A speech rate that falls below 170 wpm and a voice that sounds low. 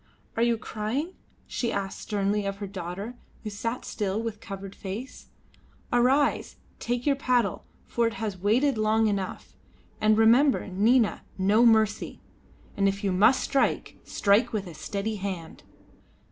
No: average, 150 wpm; high, 215 Hz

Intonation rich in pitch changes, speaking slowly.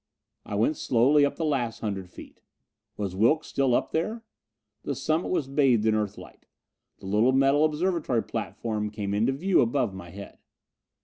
No: wide, 5.9 semitones; average, 165 wpm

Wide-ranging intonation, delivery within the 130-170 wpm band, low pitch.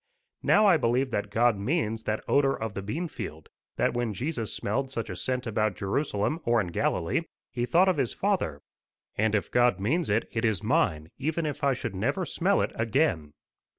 No: wide, 5.7 semitones; average, 195 wpm; low, 120 Hz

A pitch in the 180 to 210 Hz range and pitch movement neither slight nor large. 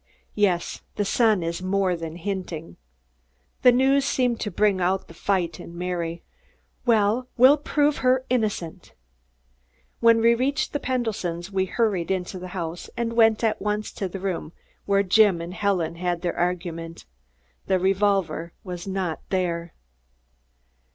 Yes: high, 190 Hz; average, 4.3 semitones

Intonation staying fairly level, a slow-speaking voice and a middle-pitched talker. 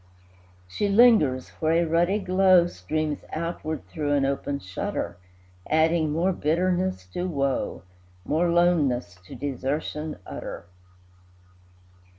No: average, 4.0 semitones; slow, 110 wpm; medium, 155 Hz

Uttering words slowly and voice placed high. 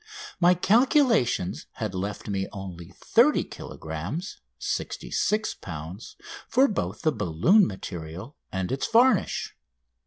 No: slow, 105 wpm; low, 105 Hz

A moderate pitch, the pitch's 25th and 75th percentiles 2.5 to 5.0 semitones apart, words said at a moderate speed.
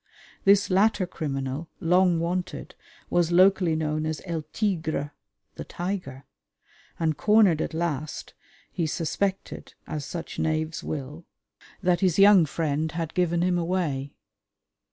No: medium, 165 Hz; average, 2.9 semitones; slow, 125 wpm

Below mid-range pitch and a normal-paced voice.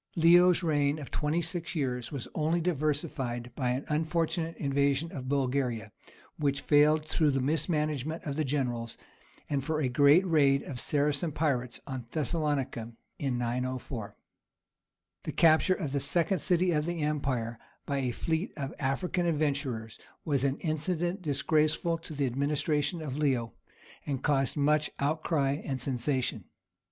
No: medium, 145 Hz; average, 145 wpm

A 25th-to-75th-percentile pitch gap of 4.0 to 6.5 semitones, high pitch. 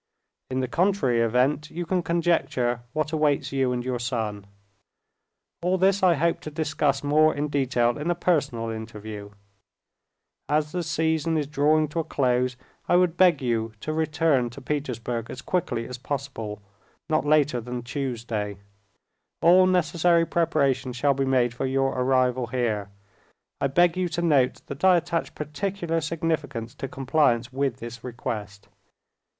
No: average, 4.8 semitones; medium, 140 Hz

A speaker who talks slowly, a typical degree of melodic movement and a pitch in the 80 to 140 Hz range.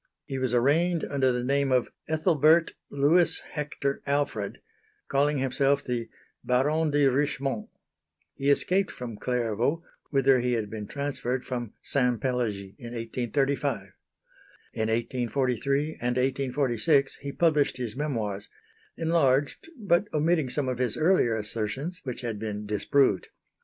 Yes: slow, 130 wpm; average, 3.3 semitones; low, 135 Hz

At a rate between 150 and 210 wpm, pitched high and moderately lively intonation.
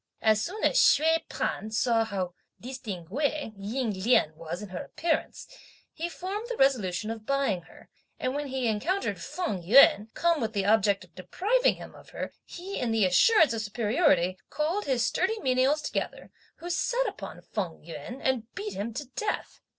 No: average, 175 wpm; high, 245 Hz; wide, 7.5 semitones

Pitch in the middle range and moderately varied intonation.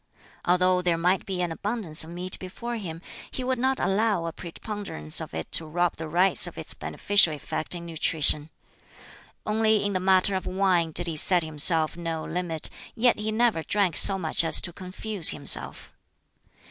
Yes: medium, 180 Hz; average, 3.7 semitones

